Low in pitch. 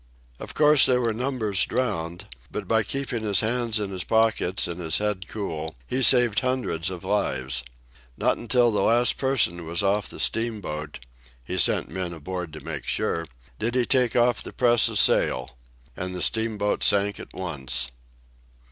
Yes: low, 100 Hz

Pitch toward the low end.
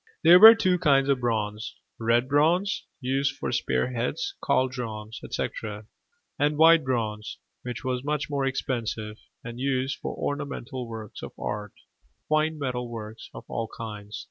Yes: low, 125 Hz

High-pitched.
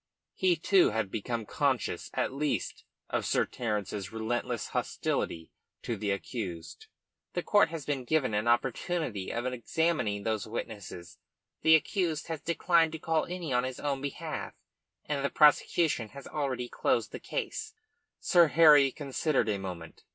No: low, 130 Hz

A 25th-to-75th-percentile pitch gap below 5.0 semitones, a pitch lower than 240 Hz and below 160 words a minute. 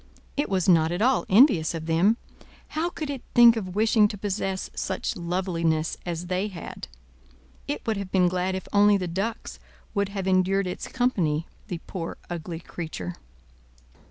No: average, 3.4 semitones; high, 190 Hz; average, 165 wpm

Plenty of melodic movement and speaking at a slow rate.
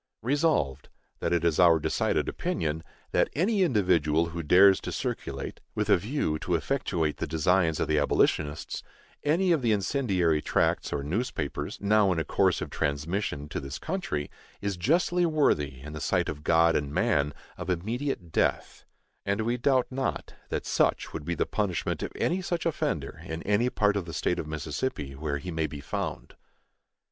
No: wide, 8.0 semitones; average, 175 wpm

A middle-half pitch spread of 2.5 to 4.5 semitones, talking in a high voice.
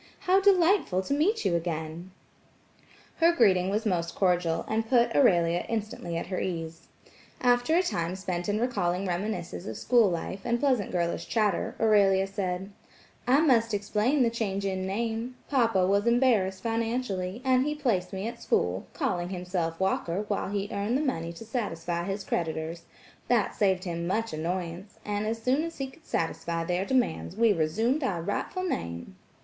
No: average, 5.2 semitones; high, 200 Hz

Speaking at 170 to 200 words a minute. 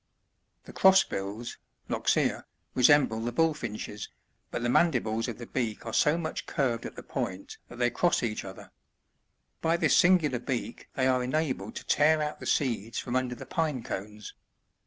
Yes: average, 175 wpm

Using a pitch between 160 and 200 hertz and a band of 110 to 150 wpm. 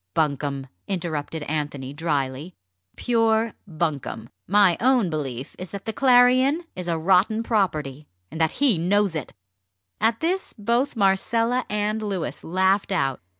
Yes: high, 190 Hz; slow, 135 wpm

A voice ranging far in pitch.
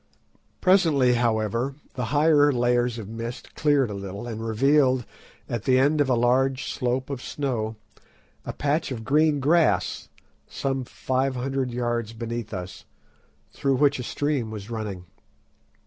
No: average, 3.3 semitones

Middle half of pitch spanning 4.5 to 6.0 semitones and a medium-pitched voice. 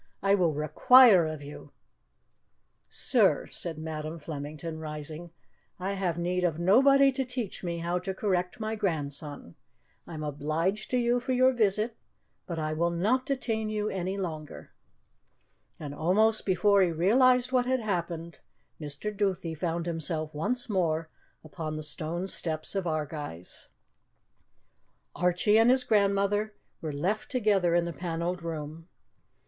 Yes: average, 5.2 semitones; medium, 175 Hz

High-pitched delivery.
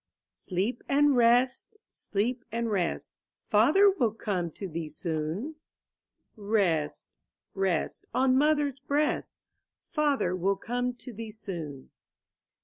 Yes: high, 225 Hz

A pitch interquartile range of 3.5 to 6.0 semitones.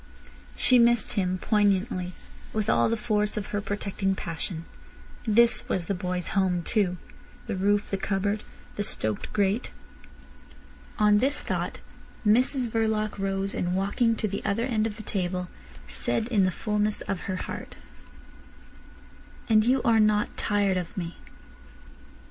No: narrow, 2.4 semitones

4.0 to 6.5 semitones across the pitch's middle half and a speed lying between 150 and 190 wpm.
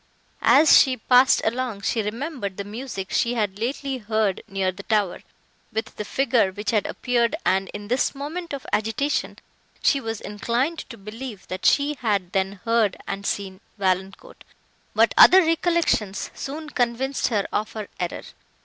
Yes: average, 5.0 semitones; average, 160 wpm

